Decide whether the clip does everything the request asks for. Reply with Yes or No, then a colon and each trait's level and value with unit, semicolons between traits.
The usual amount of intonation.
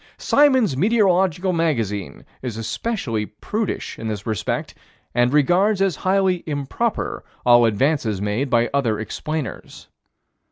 No: wide, 8.9 semitones